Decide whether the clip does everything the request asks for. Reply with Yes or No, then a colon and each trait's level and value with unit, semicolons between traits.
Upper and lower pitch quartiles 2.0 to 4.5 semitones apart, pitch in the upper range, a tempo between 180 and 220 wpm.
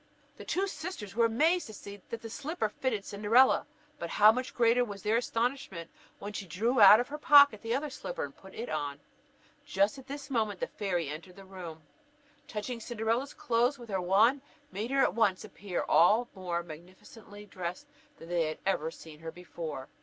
No: average, 5.2 semitones; high, 210 Hz; average, 195 wpm